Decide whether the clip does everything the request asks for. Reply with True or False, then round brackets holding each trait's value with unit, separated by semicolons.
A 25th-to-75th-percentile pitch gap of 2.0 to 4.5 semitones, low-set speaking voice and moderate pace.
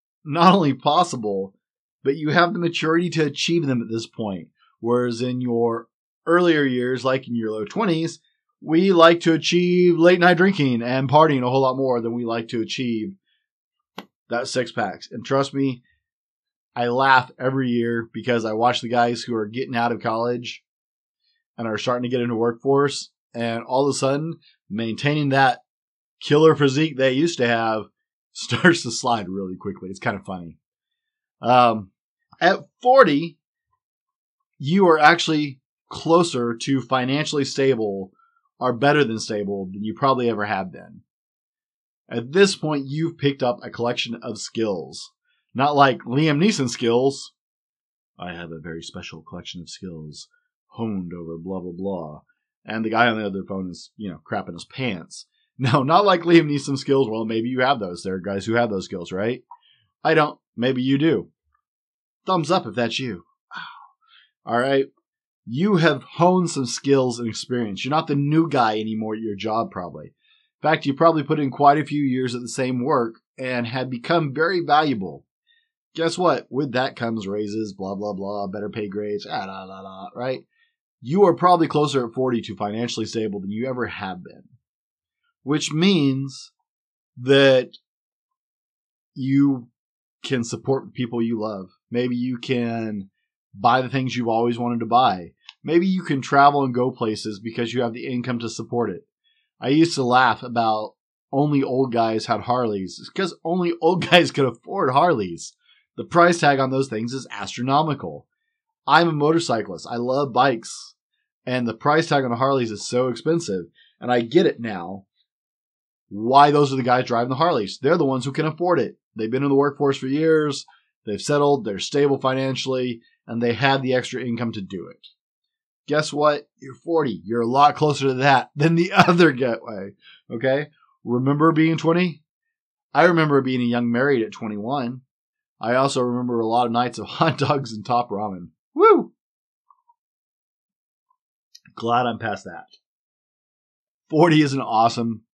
False (5.5 semitones; 130 Hz; 175 wpm)